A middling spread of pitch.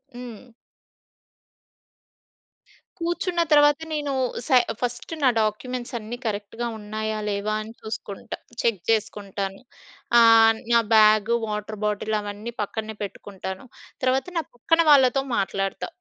Yes: average, 3.1 semitones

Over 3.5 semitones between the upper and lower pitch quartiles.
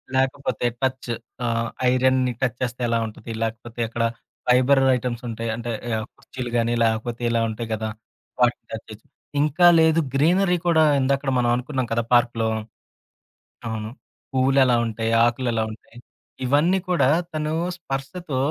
No: average, 2.8 semitones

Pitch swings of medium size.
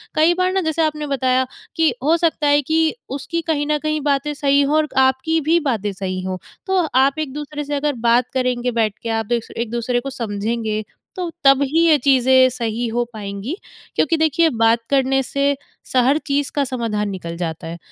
Yes: average, 4.4 semitones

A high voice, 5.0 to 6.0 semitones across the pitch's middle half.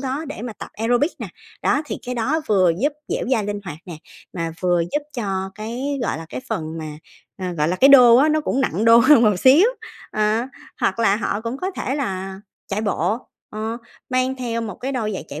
Yes: high, 225 Hz; average, 5.3 semitones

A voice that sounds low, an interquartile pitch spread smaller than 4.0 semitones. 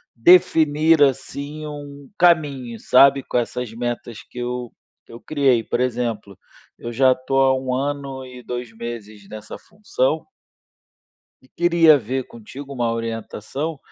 Yes: low, 130 Hz; average, 3.5 semitones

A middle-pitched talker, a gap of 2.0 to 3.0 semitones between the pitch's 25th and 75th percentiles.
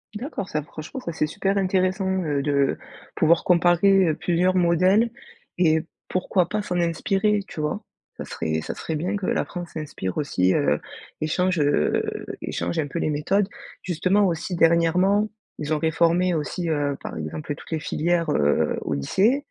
No: medium, 170 Hz; average, 3.7 semitones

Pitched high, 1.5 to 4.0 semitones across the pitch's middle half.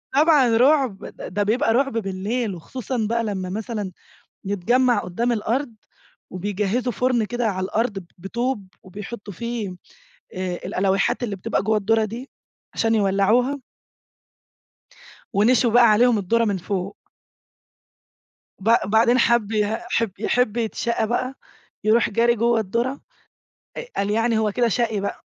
Yes: high, 225 Hz; average, 3.1 semitones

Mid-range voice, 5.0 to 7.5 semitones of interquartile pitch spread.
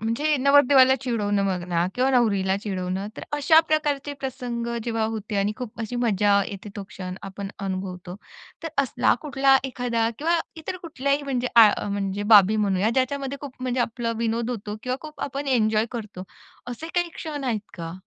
No: high, 235 Hz; average, 5.3 semitones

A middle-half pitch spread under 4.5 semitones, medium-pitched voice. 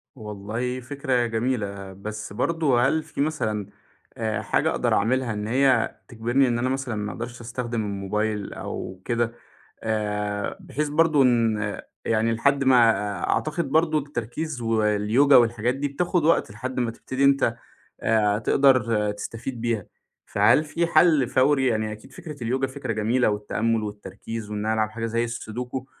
No: average, 3.7 semitones; low, 115 Hz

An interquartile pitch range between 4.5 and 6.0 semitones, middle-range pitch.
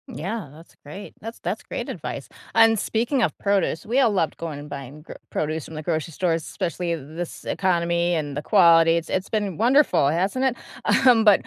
Yes: average, 4.9 semitones; medium, 175 Hz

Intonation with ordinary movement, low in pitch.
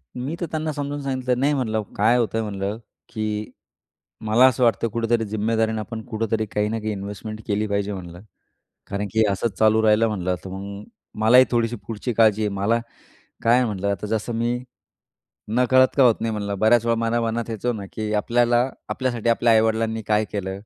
No: narrow, 2.1 semitones; low, 110 Hz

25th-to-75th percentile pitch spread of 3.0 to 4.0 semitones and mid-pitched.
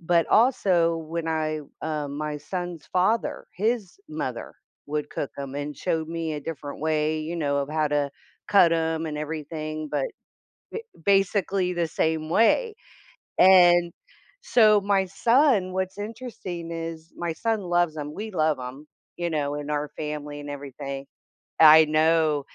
Yes: average, 3.3 semitones; medium, 160 Hz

